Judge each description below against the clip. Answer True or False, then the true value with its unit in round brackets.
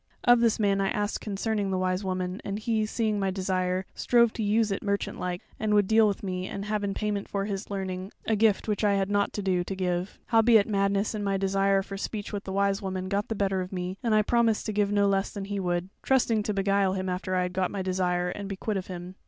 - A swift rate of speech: True (260 wpm)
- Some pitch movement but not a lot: False (2.0 semitones)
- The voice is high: True (200 Hz)